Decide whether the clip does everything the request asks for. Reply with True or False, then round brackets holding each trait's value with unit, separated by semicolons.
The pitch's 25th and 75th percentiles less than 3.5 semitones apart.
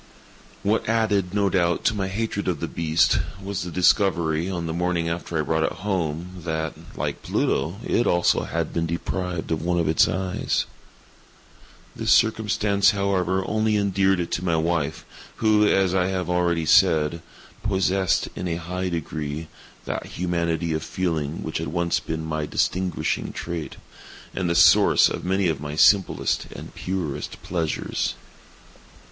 True (2.8 semitones)